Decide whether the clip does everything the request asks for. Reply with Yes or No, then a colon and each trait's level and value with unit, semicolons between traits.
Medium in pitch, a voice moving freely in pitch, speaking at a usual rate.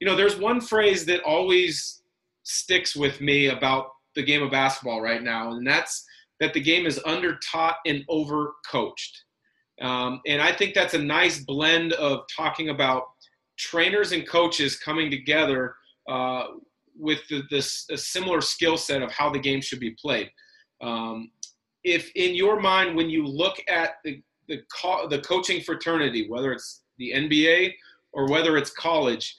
No: medium, 155 Hz; average, 4.5 semitones; average, 165 wpm